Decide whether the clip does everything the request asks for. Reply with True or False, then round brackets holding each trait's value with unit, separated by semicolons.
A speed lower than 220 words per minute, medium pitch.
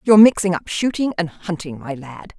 True (200 wpm; 180 Hz)